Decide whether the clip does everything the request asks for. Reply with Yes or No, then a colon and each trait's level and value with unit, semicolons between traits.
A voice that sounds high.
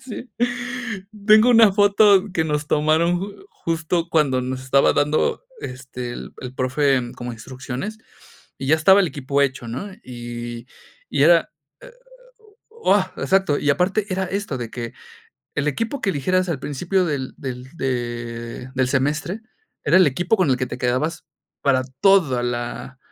No: medium, 145 Hz